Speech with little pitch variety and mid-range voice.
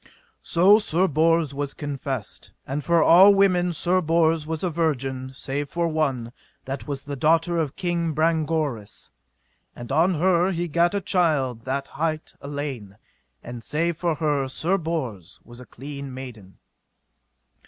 No: average, 4.0 semitones; medium, 155 Hz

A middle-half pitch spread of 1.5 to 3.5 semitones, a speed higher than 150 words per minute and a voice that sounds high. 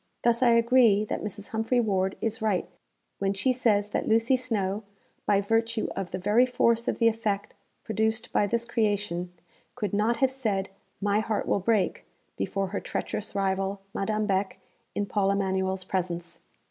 Yes: average, 2.7 semitones; average, 165 wpm; high, 210 Hz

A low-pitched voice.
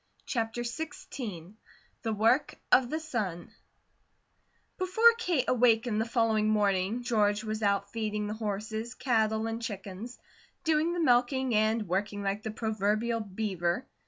No: high, 220 Hz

